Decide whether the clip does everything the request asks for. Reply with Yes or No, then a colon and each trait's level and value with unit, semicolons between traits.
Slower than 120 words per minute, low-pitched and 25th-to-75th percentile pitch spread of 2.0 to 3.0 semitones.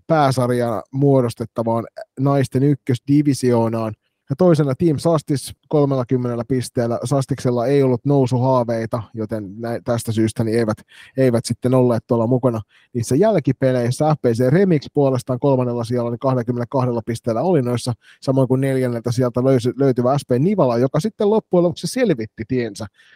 No: average, 130 wpm; low, 125 Hz; average, 2.7 semitones